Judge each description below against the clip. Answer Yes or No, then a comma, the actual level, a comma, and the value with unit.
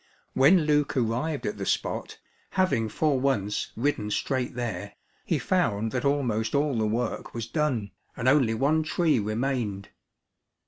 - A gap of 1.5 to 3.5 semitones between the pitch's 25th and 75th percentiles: No, average, 4.8 semitones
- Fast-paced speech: No, average, 145 wpm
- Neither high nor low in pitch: No, low, 125 Hz